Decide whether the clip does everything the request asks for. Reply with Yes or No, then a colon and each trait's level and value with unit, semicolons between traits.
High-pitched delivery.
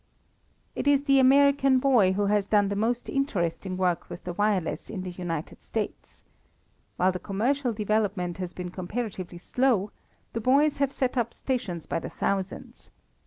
Yes: high, 205 Hz